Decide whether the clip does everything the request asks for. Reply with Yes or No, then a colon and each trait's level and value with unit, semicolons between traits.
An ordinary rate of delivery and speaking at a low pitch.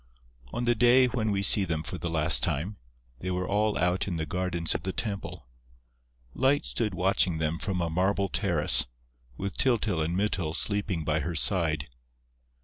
Yes: average, 175 wpm; very low, 90 Hz